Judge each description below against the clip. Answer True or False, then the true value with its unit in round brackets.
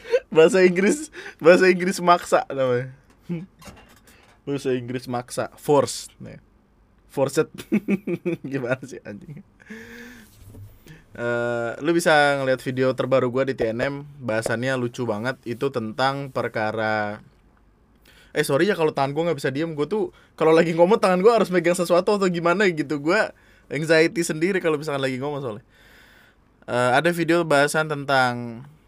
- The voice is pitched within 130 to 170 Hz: True (140 Hz)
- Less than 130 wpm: False (135 wpm)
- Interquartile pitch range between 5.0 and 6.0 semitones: True (5.3 semitones)